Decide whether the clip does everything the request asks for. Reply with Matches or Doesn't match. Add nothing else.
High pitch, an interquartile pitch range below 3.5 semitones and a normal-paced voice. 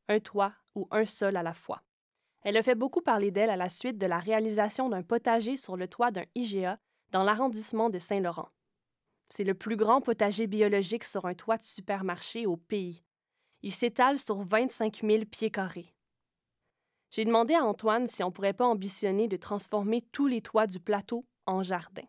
Matches